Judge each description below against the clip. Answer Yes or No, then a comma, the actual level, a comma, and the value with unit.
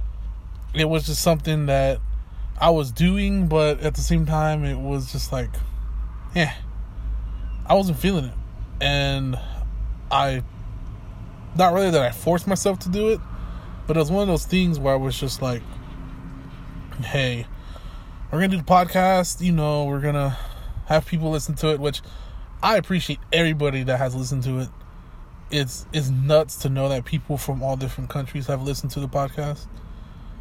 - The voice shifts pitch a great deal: Yes, wide, 6.3 semitones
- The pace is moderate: Yes, average, 170 wpm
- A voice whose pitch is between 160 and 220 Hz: No, medium, 140 Hz